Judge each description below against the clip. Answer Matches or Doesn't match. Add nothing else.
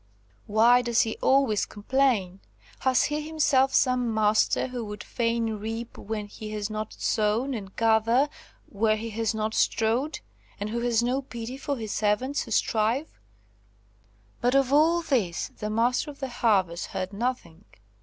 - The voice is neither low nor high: Doesn't match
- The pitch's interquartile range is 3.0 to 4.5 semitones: Matches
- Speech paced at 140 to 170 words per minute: Matches